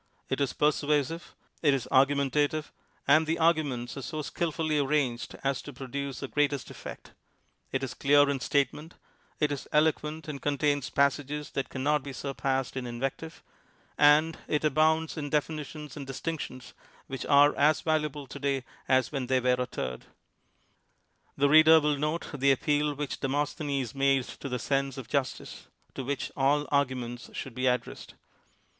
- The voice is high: No, medium, 140 Hz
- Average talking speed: Yes, average, 160 wpm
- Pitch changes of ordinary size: No, narrow, 2.1 semitones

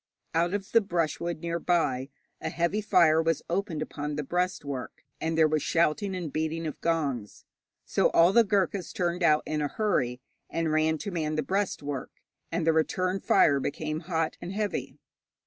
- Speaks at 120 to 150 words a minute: No, average, 175 wpm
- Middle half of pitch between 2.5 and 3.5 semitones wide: Yes, average, 2.9 semitones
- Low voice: No, medium, 165 Hz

